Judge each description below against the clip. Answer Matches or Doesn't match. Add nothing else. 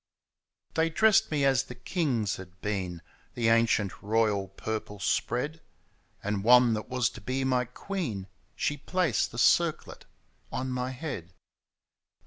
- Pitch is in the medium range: Doesn't match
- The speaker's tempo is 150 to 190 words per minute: Doesn't match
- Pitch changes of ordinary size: Matches